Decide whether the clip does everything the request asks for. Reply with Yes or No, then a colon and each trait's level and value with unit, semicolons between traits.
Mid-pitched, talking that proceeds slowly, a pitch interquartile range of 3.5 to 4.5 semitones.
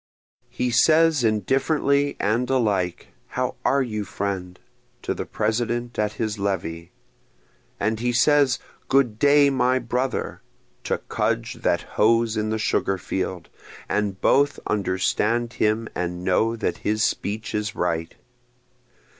No: low, 110 Hz; slow, 130 wpm; average, 3.9 semitones